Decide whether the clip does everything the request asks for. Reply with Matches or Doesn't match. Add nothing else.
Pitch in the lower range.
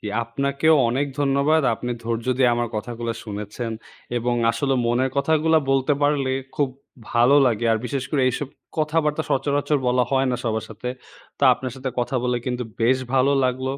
Matches